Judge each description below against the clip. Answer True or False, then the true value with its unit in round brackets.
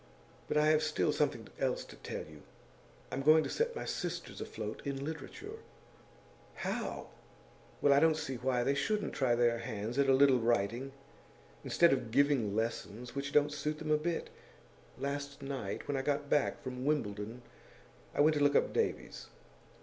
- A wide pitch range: False (3.8 semitones)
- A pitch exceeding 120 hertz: True (140 Hz)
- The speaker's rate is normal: True (175 wpm)